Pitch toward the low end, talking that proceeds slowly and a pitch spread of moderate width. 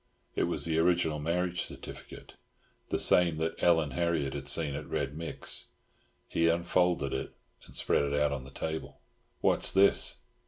No: very low, 80 Hz; average, 160 wpm; average, 3.1 semitones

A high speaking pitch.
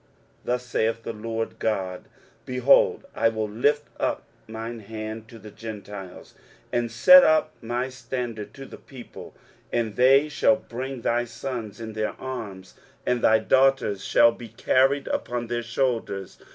No: low, 115 Hz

